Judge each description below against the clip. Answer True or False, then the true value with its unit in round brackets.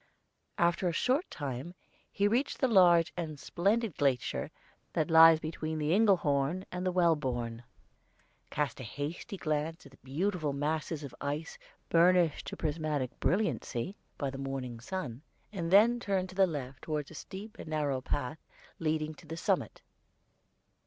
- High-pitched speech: False (160 Hz)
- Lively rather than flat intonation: False (4.3 semitones)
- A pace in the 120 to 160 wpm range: True (150 wpm)